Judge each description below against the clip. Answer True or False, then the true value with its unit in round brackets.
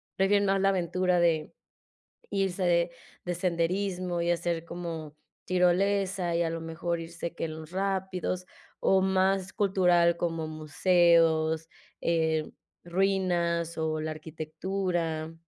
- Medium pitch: True (175 Hz)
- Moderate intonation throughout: False (2.3 semitones)